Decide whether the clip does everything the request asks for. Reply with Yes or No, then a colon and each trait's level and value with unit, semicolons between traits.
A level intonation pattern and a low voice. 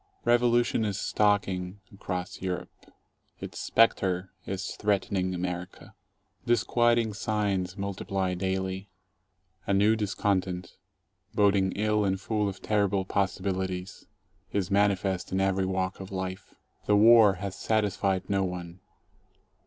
Yes: narrow, 1.8 semitones; very low, 95 Hz